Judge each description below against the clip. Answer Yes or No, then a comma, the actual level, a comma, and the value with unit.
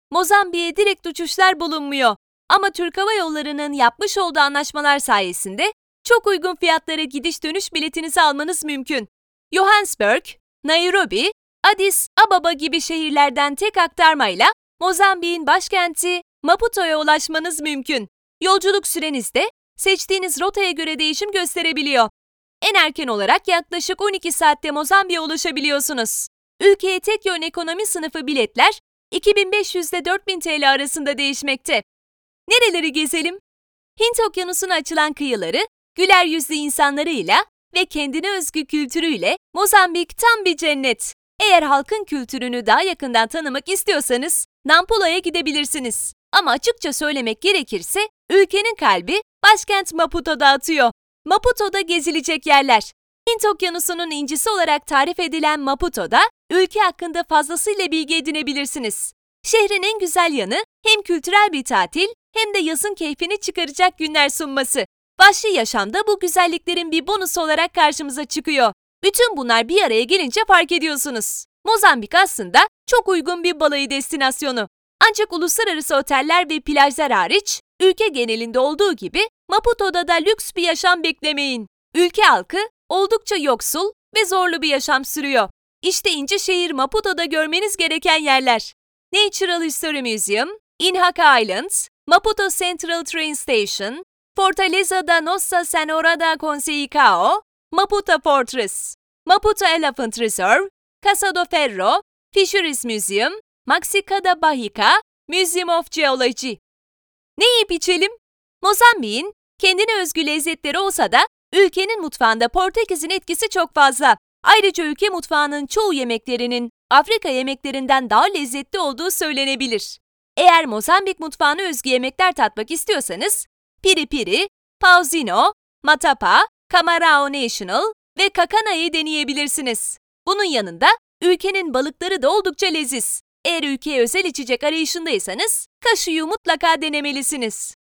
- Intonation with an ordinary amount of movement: Yes, average, 4.7 semitones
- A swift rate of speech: No, average, 115 wpm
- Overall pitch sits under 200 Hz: No, very high, 340 Hz